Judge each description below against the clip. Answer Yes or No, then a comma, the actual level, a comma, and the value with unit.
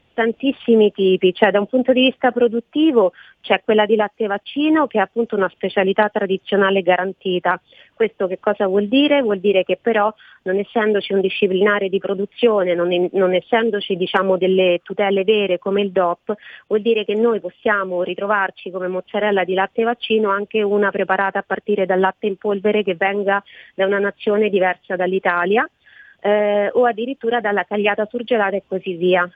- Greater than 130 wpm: Yes, fast, 170 wpm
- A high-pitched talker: Yes, high, 200 Hz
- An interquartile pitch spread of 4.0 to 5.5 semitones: No, narrow, 2.4 semitones